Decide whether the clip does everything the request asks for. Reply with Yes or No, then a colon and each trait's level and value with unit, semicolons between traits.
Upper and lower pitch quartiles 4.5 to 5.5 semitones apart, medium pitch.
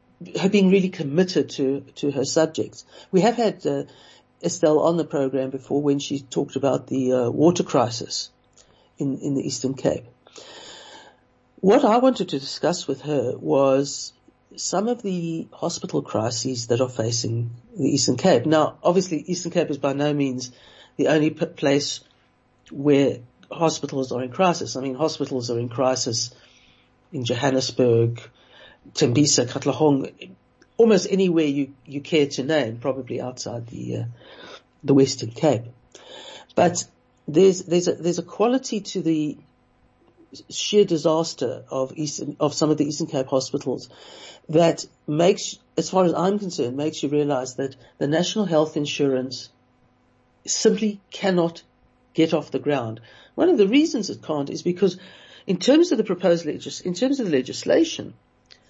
Yes: average, 5.0 semitones; medium, 145 Hz